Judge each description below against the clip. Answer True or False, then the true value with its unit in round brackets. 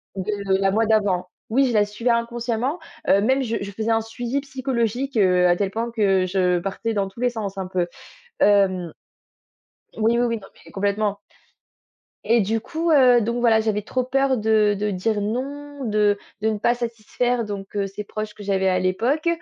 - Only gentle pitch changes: False (3.2 semitones)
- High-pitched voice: True (220 Hz)